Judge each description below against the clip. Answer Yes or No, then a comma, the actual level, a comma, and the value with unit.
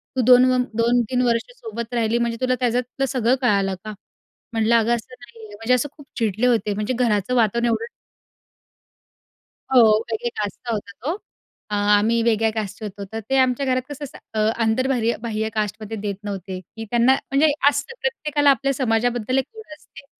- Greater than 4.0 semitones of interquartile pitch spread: No, average, 2.8 semitones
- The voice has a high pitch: Yes, high, 235 Hz